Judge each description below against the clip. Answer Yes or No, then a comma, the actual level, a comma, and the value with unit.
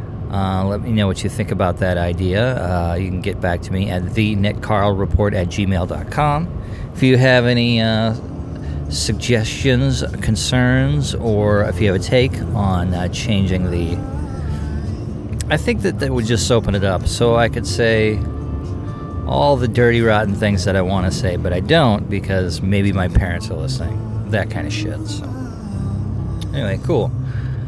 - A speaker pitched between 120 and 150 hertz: No, low, 105 Hz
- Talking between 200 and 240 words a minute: No, average, 175 wpm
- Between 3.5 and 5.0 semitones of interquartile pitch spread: Yes, average, 4.0 semitones